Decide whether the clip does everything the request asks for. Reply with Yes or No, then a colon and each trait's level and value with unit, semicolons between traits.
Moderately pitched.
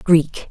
Yes: medium, 165 Hz